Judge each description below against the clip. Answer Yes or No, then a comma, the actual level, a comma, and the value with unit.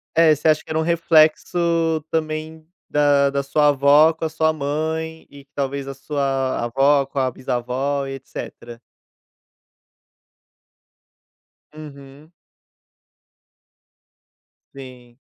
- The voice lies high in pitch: No, medium, 145 Hz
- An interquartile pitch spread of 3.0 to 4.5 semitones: No, narrow, 2.6 semitones